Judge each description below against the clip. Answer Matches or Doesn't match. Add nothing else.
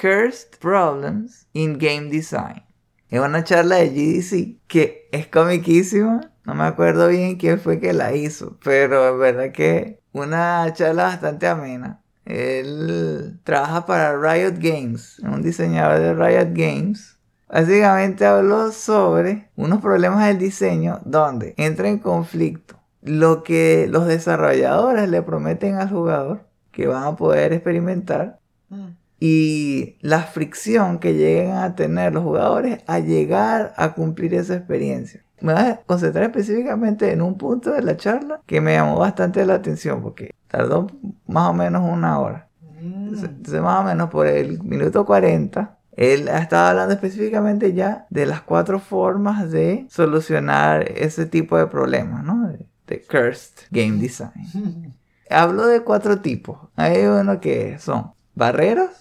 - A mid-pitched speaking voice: Matches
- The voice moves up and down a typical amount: Doesn't match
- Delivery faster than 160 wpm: Doesn't match